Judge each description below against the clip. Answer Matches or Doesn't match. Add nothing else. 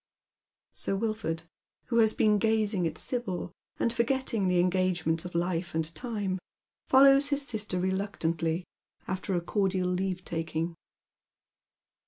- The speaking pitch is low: Doesn't match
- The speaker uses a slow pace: Matches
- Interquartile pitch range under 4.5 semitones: Matches